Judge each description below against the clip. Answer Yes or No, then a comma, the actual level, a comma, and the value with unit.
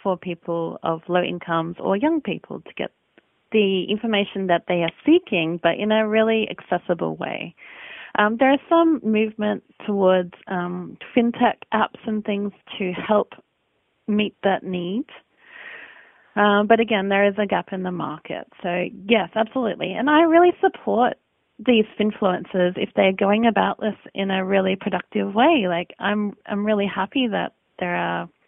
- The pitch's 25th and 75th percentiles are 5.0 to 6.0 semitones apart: No, average, 3.4 semitones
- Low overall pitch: No, high, 205 Hz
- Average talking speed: Yes, average, 160 wpm